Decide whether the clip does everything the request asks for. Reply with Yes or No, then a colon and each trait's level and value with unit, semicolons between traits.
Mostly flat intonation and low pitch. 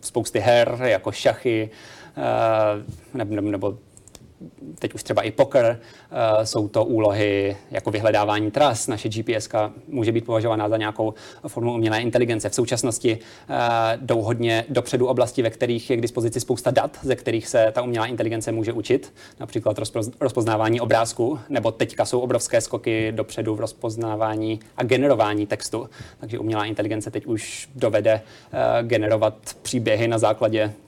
Yes: narrow, 1.6 semitones; low, 110 Hz